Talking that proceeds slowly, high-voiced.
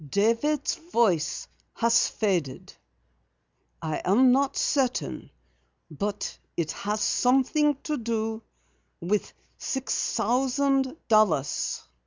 Yes: slow, 90 wpm; high, 230 Hz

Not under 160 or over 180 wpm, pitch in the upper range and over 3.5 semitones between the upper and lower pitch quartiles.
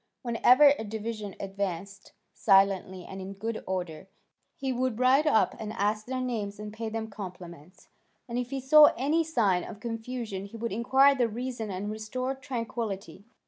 Yes: average, 165 wpm; high, 220 Hz; average, 4.1 semitones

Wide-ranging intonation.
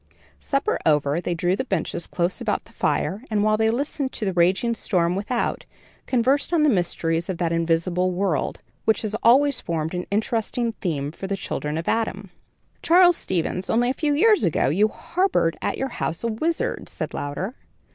Yes: wide, 6.1 semitones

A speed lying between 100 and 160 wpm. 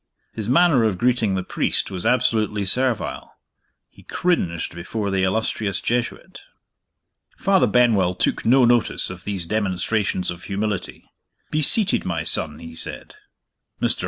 Yes: slow, 135 wpm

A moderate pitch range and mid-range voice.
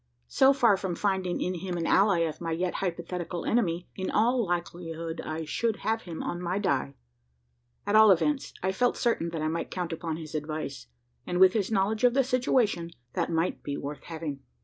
Yes: average, 4.2 semitones; medium, 180 Hz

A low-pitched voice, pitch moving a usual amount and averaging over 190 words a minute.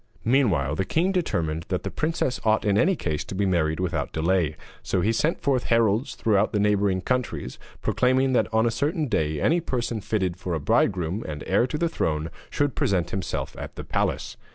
No: low, 105 Hz; wide, 6.7 semitones; average, 200 wpm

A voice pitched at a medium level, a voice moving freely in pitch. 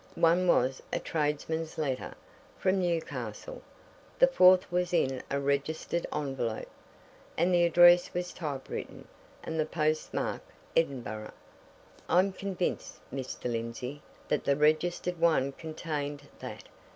No: medium, 155 Hz; average, 4.0 semitones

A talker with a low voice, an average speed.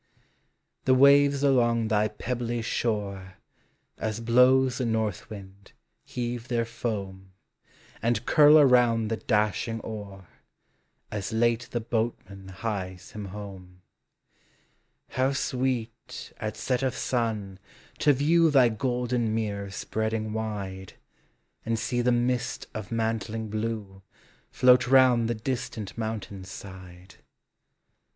No: low, 115 Hz; slow, 115 wpm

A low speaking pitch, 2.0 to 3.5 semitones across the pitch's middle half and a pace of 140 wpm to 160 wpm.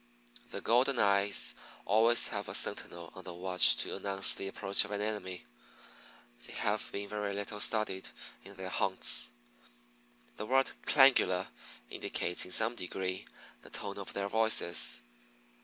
Yes: low, 100 Hz; narrow, 2.6 semitones; average, 145 wpm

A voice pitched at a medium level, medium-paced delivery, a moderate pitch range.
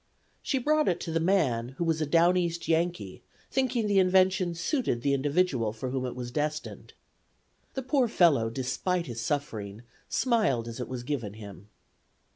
No: medium, 155 Hz; average, 170 wpm; wide, 7.2 semitones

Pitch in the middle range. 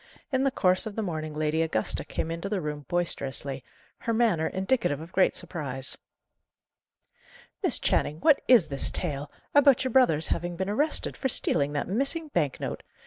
Yes: medium, 175 Hz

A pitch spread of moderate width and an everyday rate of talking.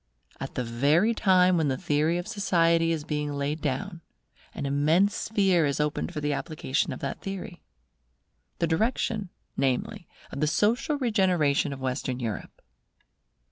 Yes: average, 4.9 semitones; average, 150 wpm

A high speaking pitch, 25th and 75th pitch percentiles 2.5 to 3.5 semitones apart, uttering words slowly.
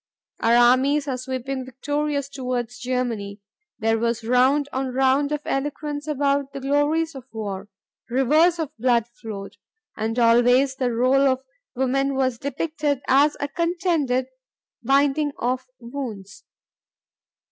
Yes: very high, 265 Hz; average, 2.8 semitones; slow, 125 wpm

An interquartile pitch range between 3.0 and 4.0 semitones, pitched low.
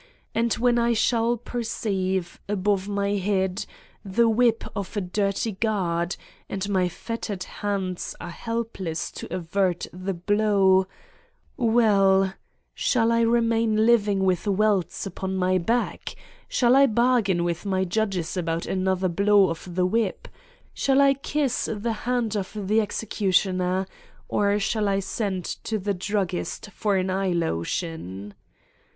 No: average, 3.3 semitones; high, 200 Hz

